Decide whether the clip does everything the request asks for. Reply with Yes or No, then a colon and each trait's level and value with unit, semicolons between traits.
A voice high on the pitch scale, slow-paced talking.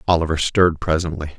No: very low, 80 Hz; slow, 130 wpm